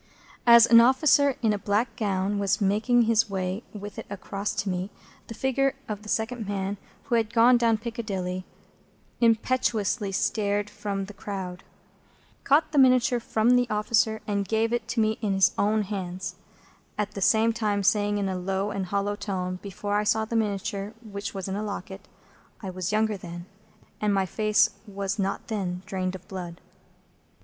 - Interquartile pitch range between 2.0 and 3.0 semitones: Yes, narrow, 2.5 semitones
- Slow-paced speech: No, average, 175 wpm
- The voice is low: No, high, 205 Hz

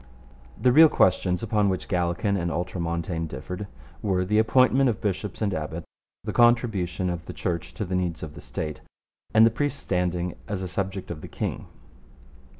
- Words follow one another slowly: No, average, 175 wpm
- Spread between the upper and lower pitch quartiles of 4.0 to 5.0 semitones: No, average, 3.6 semitones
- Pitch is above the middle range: No, very low, 95 Hz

